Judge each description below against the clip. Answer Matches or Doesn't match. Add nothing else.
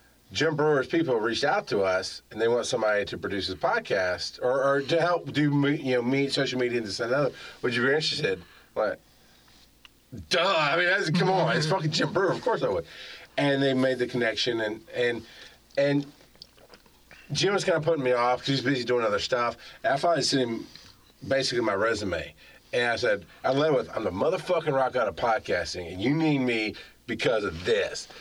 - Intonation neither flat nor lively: Matches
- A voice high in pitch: Doesn't match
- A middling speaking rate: Doesn't match